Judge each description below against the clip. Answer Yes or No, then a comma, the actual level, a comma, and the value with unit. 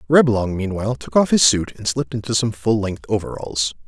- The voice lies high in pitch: No, low, 110 Hz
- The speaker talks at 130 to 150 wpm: No, average, 200 wpm